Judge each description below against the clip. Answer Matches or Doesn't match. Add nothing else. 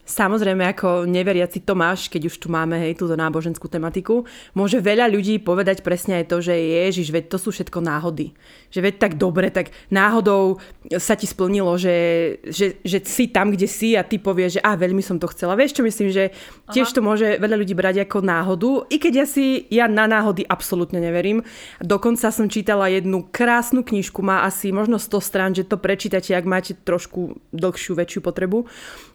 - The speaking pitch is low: Doesn't match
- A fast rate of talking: Matches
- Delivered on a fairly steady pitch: Doesn't match